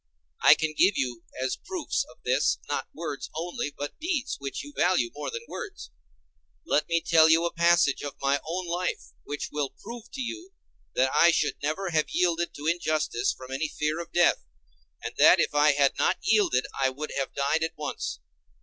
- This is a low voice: No, medium, 160 Hz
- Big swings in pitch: No, average, 3.7 semitones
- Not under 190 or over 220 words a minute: Yes, average, 195 wpm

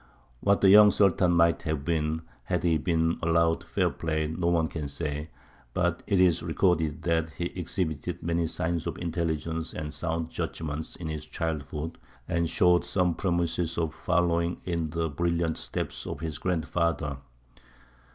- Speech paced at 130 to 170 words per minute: Yes, average, 155 wpm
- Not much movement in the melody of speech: Yes, narrow, 1.7 semitones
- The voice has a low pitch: Yes, very low, 85 Hz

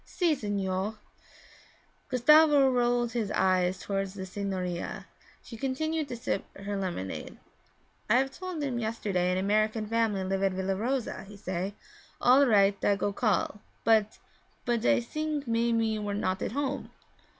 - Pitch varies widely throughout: No, average, 4.3 semitones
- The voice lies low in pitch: No, high, 215 Hz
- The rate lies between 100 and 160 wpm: Yes, average, 150 wpm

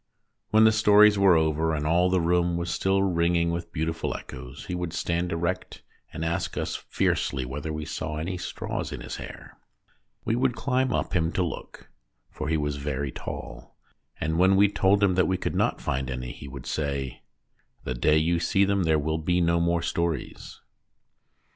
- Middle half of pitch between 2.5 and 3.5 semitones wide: Yes, average, 3.1 semitones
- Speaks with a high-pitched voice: No, very low, 85 Hz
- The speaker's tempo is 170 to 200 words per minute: Yes, average, 190 wpm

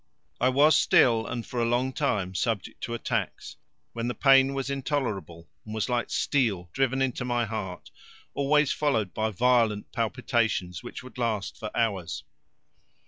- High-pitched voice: No, low, 120 Hz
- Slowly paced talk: No, average, 155 wpm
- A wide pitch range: No, average, 3.6 semitones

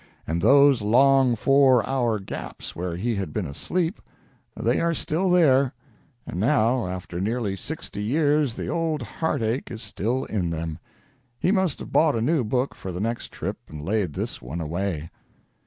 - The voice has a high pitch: No, low, 115 Hz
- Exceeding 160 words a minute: Yes, average, 170 wpm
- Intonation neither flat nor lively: No, wide, 6.7 semitones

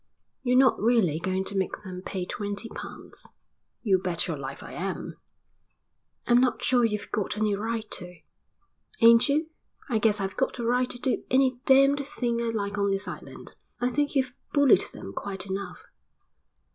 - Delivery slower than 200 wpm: Yes, average, 175 wpm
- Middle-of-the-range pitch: No, high, 220 Hz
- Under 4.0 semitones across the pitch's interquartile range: No, average, 4.4 semitones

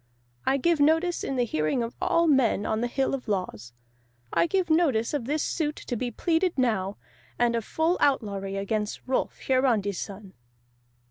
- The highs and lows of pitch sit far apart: Yes, wide, 6.3 semitones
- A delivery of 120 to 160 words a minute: No, average, 175 wpm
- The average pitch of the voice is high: Yes, high, 245 Hz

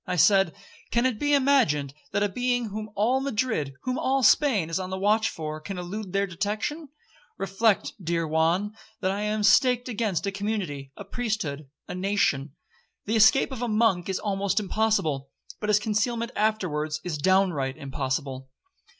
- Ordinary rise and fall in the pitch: Yes, average, 5.0 semitones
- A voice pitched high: Yes, high, 200 Hz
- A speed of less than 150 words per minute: No, average, 165 wpm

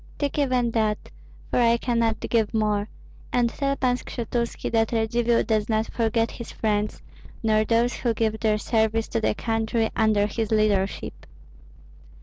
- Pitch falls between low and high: No, high, 225 Hz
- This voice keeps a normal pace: Yes, average, 150 wpm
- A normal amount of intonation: No, narrow, 1.5 semitones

